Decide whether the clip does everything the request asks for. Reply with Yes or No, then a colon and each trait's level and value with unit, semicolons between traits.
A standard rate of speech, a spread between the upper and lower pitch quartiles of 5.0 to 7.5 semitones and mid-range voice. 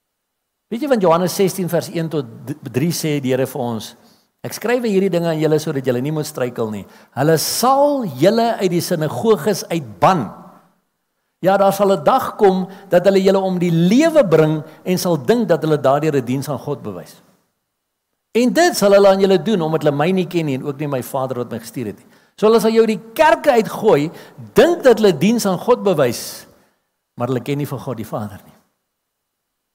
No: fast, 210 wpm; wide, 5.6 semitones; medium, 175 Hz